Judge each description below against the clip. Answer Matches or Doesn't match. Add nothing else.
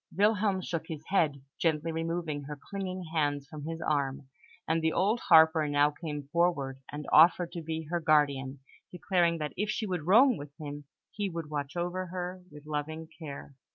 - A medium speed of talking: Matches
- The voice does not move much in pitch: Doesn't match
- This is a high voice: Doesn't match